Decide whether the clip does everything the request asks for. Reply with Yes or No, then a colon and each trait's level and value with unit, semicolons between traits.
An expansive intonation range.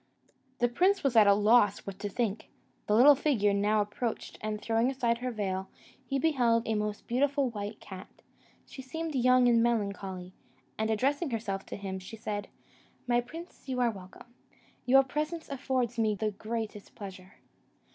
No: average, 3.8 semitones